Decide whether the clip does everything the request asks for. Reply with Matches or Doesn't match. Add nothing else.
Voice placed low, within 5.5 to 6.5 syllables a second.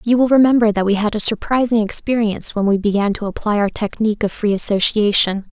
Doesn't match